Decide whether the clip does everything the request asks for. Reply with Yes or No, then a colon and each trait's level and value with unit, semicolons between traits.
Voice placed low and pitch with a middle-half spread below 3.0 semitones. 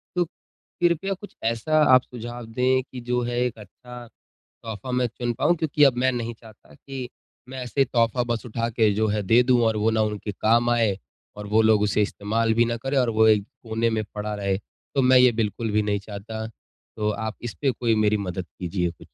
Yes: low, 115 Hz; narrow, 2.6 semitones